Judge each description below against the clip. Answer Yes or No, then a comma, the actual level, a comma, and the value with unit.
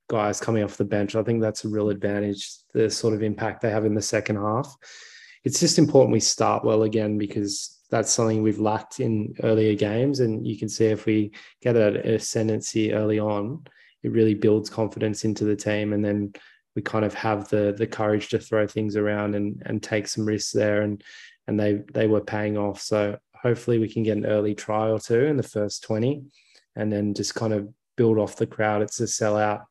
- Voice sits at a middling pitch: No, low, 110 Hz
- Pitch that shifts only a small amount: Yes, narrow, 1.1 semitones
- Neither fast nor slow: No, fast, 215 wpm